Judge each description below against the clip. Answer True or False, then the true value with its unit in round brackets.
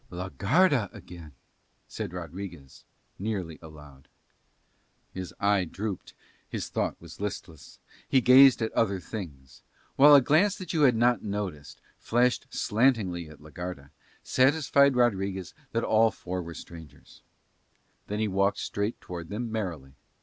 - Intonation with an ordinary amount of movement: False (5.9 semitones)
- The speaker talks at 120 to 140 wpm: True (135 wpm)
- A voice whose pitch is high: False (100 Hz)